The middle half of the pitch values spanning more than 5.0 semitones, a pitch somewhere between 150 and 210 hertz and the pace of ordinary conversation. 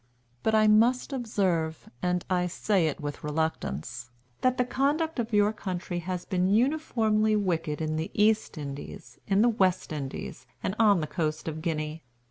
Yes: wide, 5.5 semitones; medium, 185 Hz; average, 165 wpm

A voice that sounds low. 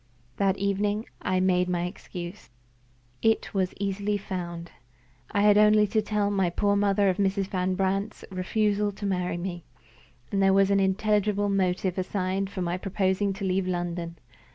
No: high, 195 Hz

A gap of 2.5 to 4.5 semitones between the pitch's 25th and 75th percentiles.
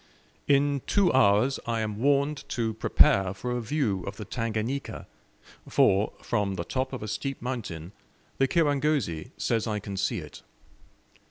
No: average, 5.3 semitones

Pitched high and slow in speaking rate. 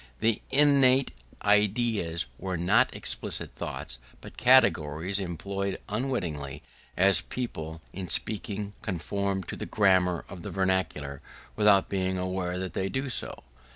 No: very low, 95 Hz; slow, 125 wpm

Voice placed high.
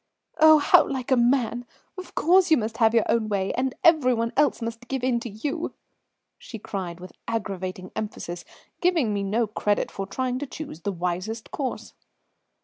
Yes: high, 230 Hz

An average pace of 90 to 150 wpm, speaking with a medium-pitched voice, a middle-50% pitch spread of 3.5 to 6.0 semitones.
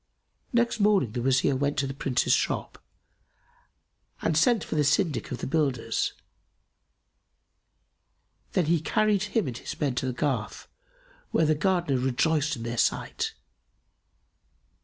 Yes: average, 140 wpm; medium, 145 Hz; average, 5.1 semitones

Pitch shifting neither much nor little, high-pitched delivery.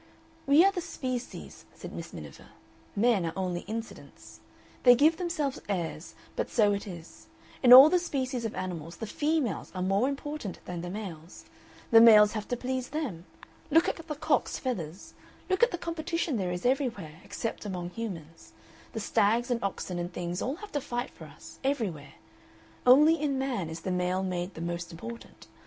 No: wide, 7.4 semitones; high, 225 Hz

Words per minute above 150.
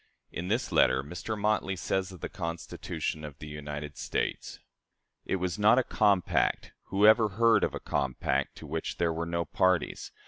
Yes: average, 175 wpm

